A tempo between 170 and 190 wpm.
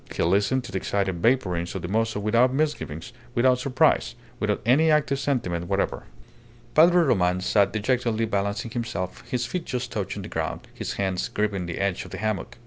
Yes: average, 180 wpm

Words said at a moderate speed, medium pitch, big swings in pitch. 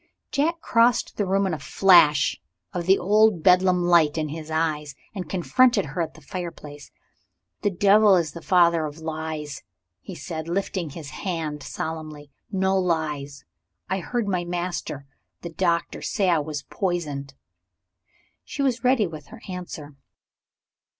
No: average, 150 wpm; medium, 170 Hz; average, 3.8 semitones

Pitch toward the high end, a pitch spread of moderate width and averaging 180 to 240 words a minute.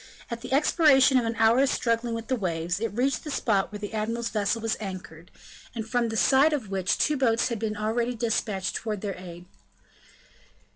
Yes: high, 225 Hz; average, 3.2 semitones; average, 195 wpm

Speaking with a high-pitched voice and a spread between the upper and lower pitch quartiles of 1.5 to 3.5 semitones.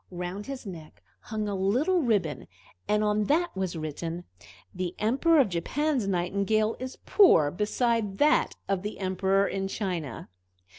No: high, 200 Hz; average, 4.3 semitones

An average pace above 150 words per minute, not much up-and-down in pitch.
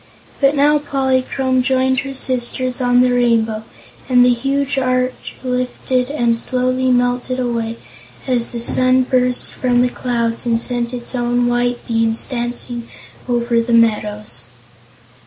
No: average, 140 wpm; narrow, 1.4 semitones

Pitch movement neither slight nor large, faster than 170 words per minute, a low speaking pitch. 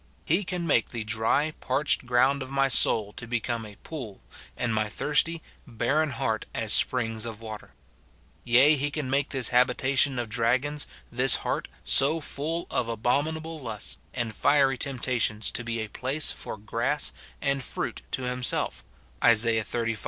No: average, 3.8 semitones; average, 165 wpm; low, 125 Hz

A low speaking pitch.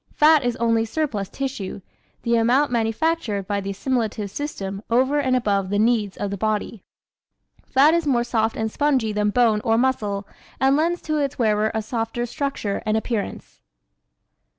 No: high, 230 Hz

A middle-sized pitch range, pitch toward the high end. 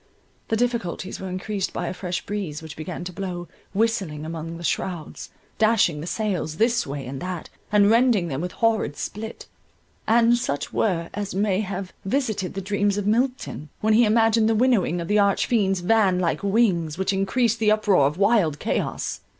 Yes: average, 4.1 semitones; high, 195 Hz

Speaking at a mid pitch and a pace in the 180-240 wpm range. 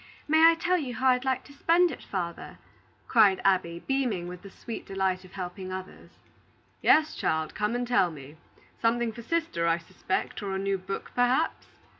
No: high, 205 Hz; average, 185 wpm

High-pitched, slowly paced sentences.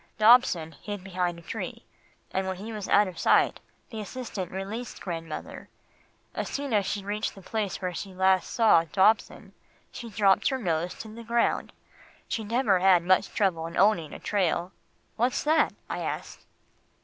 No: high, 195 Hz; average, 175 wpm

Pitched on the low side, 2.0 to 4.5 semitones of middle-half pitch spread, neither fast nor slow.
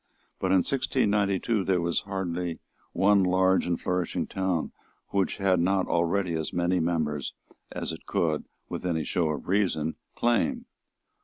Yes: very low, 90 Hz; narrow, 2.6 semitones; average, 145 wpm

